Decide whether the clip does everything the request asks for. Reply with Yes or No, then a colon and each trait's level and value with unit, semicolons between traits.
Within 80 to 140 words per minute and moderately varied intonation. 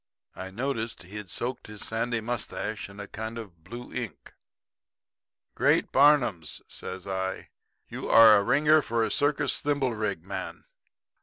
Yes: slow, 135 wpm; average, 3.8 semitones